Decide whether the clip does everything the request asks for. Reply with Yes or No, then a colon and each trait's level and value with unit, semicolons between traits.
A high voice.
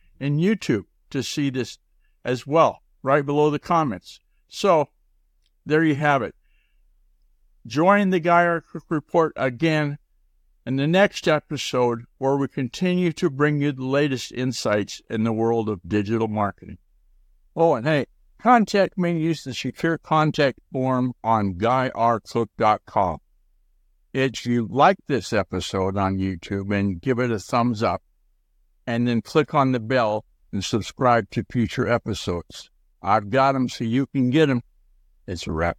No: low, 125 Hz